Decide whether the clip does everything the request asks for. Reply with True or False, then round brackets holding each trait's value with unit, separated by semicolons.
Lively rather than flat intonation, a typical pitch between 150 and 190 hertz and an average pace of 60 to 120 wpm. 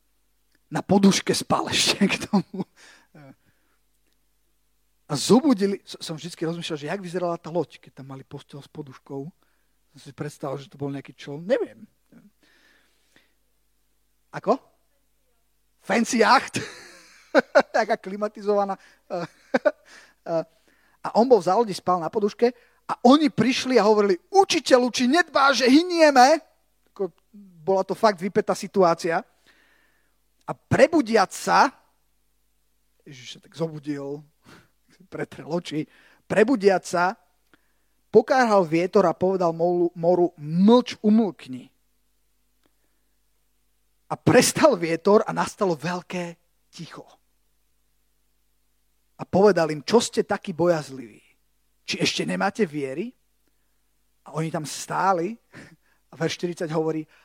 True (5.7 semitones; 185 Hz; 110 wpm)